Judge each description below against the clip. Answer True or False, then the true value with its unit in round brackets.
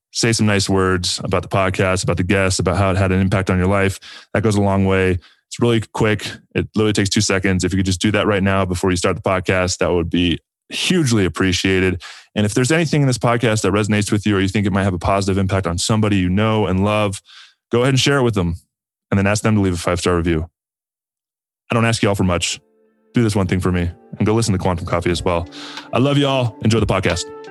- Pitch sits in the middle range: False (100 Hz)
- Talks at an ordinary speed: False (265 wpm)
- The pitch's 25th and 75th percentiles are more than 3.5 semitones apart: False (2.9 semitones)